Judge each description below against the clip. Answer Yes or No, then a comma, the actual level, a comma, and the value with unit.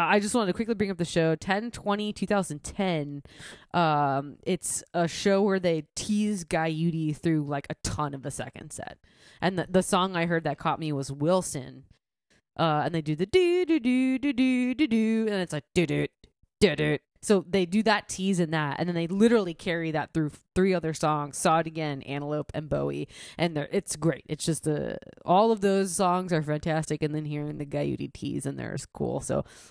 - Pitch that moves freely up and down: No, average, 4.6 semitones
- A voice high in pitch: No, medium, 165 Hz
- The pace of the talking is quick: Yes, fast, 215 wpm